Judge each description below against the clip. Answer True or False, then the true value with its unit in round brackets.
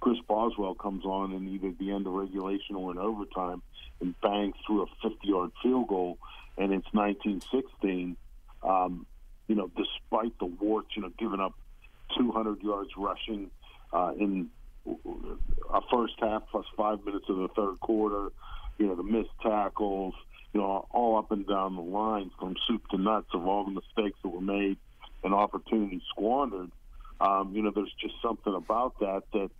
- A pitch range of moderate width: False (1.9 semitones)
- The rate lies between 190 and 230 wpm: False (175 wpm)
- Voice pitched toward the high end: False (100 Hz)